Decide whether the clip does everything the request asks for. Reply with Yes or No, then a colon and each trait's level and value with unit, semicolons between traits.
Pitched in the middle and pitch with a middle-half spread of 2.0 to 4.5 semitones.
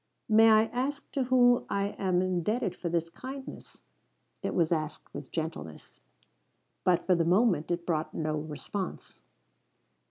No: medium, 180 Hz; wide, 5.5 semitones